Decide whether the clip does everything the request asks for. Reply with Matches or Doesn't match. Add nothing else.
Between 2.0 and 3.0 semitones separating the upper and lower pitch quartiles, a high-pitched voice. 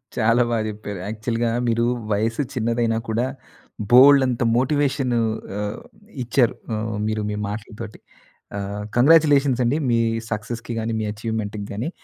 Doesn't match